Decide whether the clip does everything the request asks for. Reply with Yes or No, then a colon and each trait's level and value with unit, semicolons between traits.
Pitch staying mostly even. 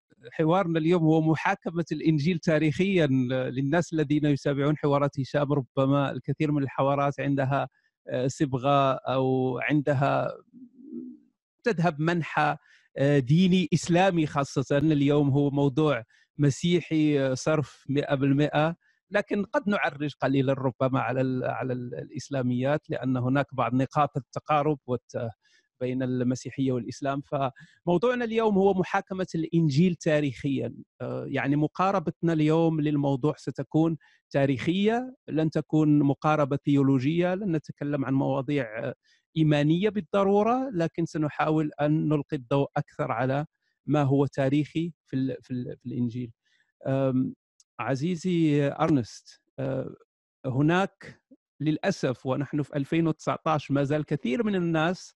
No: average, 3.2 semitones